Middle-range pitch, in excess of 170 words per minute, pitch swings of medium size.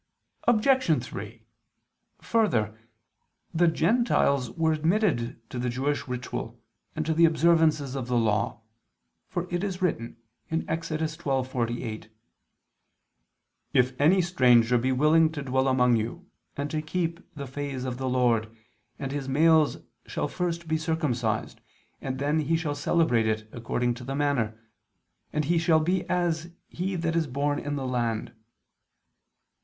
No: medium, 145 Hz; average, 140 wpm; average, 4.9 semitones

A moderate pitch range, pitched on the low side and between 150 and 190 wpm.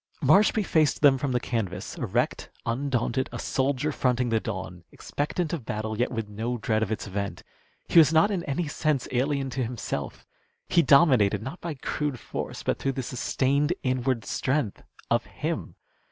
Yes: average, 4.4 semitones; low, 130 Hz; average, 170 wpm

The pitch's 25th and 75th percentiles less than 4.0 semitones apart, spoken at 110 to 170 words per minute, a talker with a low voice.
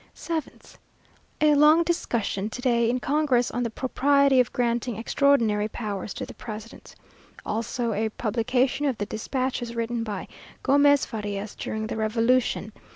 No: average, 3.6 semitones; average, 145 wpm; high, 235 Hz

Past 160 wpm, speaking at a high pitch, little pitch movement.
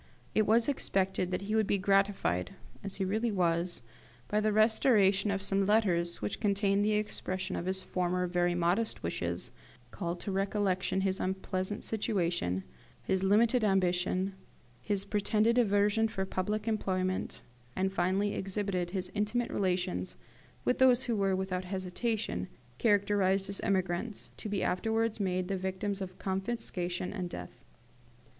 No: average, 145 wpm; high, 195 Hz; narrow, 2.3 semitones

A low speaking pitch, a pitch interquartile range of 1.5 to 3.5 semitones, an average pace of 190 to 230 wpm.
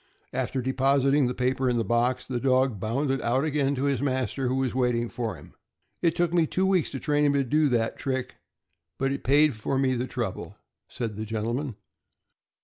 Yes: low, 130 Hz; narrow, 2.5 semitones; average, 200 wpm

